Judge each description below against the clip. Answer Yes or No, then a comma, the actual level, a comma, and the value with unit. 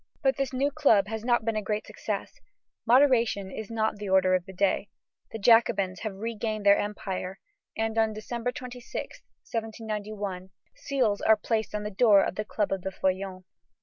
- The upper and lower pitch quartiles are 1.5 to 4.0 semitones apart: Yes, narrow, 2.6 semitones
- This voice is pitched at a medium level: No, high, 215 Hz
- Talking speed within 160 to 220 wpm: Yes, average, 180 wpm